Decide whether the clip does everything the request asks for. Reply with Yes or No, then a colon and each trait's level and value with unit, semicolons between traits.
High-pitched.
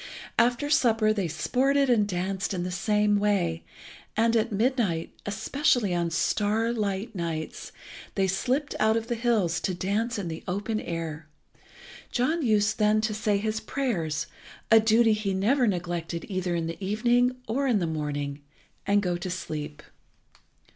Yes: high, 205 Hz